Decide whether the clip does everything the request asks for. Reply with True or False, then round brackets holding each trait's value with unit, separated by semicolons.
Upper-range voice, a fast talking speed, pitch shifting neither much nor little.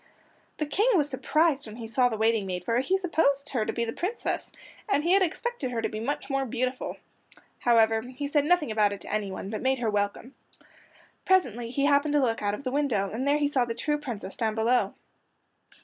True (255 Hz; 220 wpm; 4.7 semitones)